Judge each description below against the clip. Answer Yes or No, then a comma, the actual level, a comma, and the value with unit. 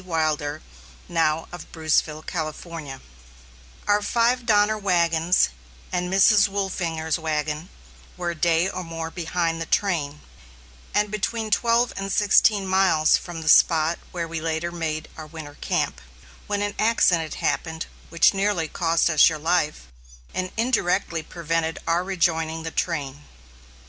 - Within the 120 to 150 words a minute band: Yes, slow, 135 wpm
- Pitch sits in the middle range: Yes, medium, 170 Hz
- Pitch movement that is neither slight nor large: Yes, average, 3.4 semitones